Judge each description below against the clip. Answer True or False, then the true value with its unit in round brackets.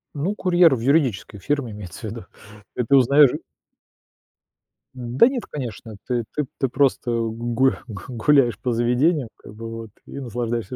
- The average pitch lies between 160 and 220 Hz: False (125 Hz)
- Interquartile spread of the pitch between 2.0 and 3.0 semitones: False (3.7 semitones)